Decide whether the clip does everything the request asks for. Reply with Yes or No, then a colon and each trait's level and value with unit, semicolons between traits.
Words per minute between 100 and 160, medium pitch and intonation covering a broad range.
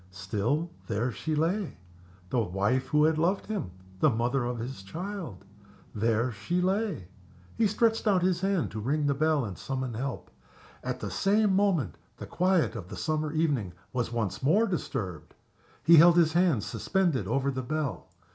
No: average, 170 wpm; medium, 145 Hz; wide, 7.3 semitones